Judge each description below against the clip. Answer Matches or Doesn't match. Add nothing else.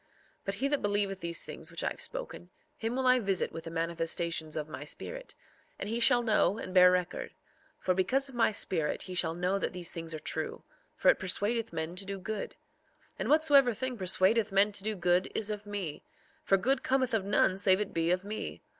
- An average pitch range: Matches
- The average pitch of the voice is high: Matches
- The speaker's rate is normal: Doesn't match